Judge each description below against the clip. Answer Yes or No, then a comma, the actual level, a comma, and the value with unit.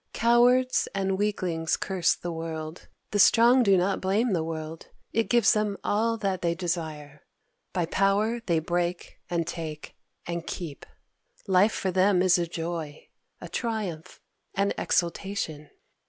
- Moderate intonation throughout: Yes, average, 3.8 semitones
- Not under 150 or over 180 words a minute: No, average, 140 wpm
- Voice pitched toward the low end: No, medium, 180 Hz